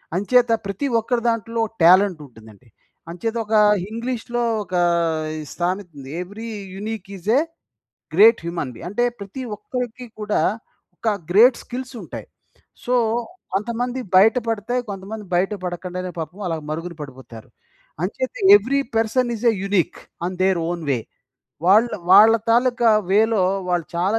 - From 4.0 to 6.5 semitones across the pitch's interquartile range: Yes, average, 4.5 semitones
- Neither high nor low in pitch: No, high, 205 Hz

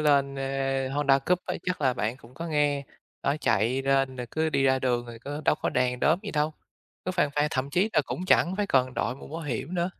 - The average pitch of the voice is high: No, medium, 140 Hz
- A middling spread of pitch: Yes, average, 3.3 semitones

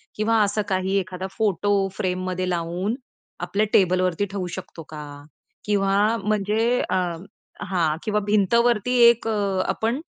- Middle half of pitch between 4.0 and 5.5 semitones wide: No, narrow, 2.6 semitones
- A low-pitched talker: No, high, 200 Hz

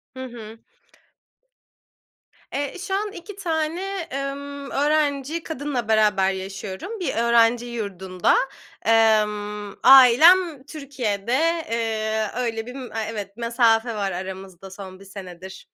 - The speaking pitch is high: Yes, high, 230 Hz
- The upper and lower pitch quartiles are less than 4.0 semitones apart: No, wide, 5.5 semitones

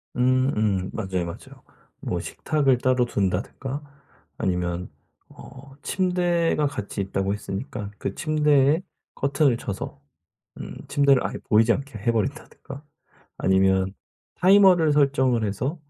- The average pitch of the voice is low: Yes, low, 130 Hz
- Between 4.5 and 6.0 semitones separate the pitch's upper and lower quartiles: No, wide, 6.5 semitones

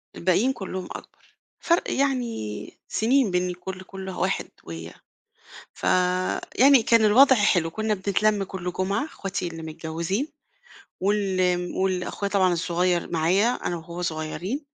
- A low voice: No, medium, 185 Hz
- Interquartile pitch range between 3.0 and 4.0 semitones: Yes, average, 3.5 semitones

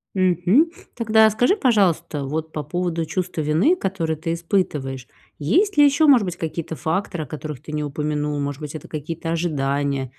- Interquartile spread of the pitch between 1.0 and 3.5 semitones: No, average, 4.5 semitones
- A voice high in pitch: No, medium, 165 Hz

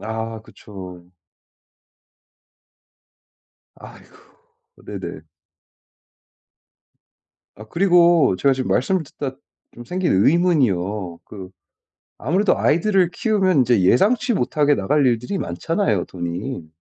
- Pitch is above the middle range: No, low, 130 Hz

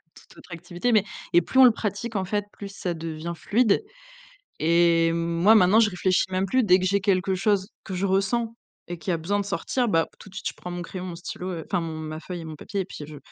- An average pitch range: Yes, average, 3.1 semitones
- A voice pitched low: No, medium, 185 Hz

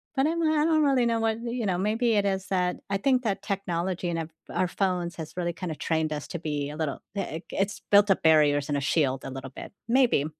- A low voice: No, medium, 185 Hz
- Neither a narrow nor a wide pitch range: No, wide, 5.9 semitones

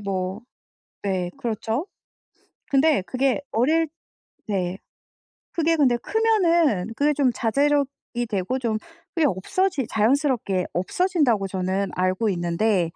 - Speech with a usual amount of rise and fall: No, wide, 7.2 semitones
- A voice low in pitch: No, high, 235 Hz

